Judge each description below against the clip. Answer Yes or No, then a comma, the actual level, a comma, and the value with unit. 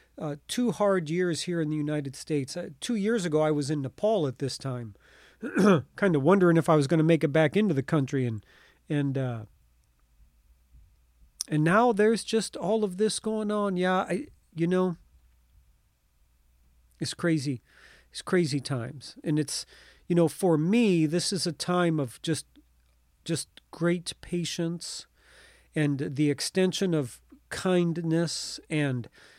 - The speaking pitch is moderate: Yes, medium, 155 Hz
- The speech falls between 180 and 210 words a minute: No, average, 155 wpm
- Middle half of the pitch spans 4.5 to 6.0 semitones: Yes, wide, 5.6 semitones